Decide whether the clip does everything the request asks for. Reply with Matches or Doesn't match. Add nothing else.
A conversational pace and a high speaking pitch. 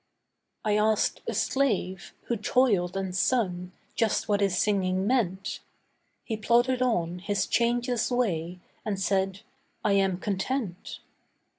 Doesn't match